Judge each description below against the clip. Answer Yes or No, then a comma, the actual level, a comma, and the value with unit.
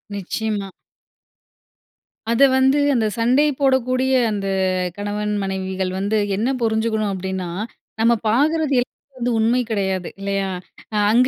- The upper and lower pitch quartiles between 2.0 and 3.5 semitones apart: No, average, 4.2 semitones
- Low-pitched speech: No, high, 220 Hz